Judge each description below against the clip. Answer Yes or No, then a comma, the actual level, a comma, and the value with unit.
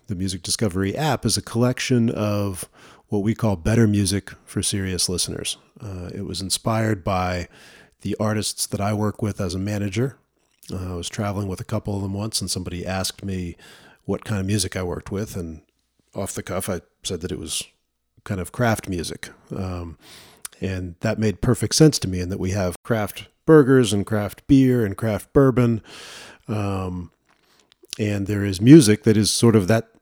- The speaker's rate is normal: Yes, average, 190 wpm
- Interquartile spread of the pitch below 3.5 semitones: Yes, average, 2.8 semitones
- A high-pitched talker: No, low, 100 Hz